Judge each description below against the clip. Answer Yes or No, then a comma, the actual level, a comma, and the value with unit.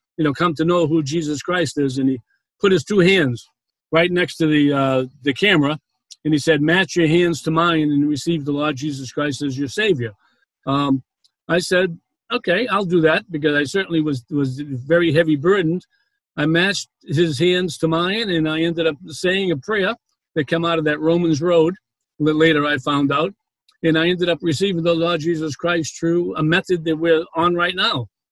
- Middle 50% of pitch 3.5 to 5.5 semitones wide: No, average, 2.9 semitones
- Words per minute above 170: Yes, fast, 205 wpm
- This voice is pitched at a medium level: Yes, medium, 160 Hz